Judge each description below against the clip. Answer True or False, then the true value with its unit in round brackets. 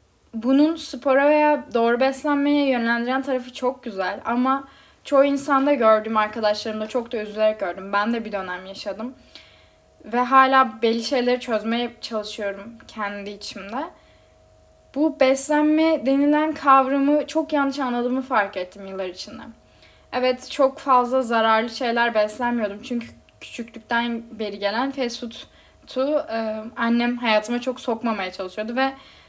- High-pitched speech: True (240 Hz)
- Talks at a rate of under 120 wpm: False (125 wpm)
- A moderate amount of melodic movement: True (3.7 semitones)